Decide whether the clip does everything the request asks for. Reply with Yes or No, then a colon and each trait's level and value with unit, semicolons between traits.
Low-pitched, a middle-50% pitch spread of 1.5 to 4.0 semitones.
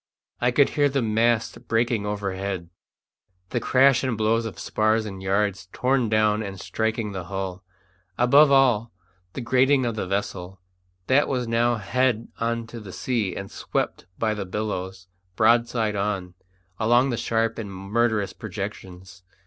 Yes: low, 110 Hz; average, 3.4 semitones